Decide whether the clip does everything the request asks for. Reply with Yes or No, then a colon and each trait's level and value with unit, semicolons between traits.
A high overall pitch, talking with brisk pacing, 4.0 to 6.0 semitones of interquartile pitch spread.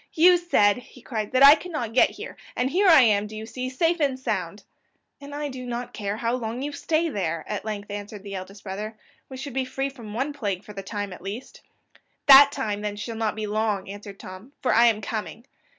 Yes: high, 225 Hz; fast, 230 wpm; average, 4.7 semitones